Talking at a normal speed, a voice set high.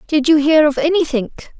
Yes: average, 190 wpm; very high, 295 Hz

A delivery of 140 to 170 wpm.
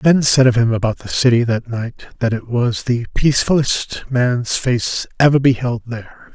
No: average, 180 wpm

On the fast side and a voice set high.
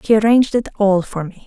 Yes: fast, 245 wpm; high, 210 Hz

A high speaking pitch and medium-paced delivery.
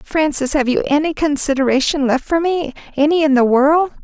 Yes: very high, 290 Hz; average, 165 wpm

